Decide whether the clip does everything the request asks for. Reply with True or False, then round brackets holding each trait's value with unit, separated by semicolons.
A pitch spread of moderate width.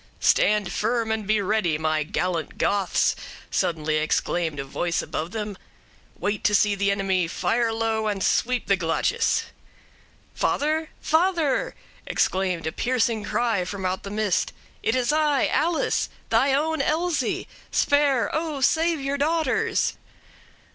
False (7.1 semitones)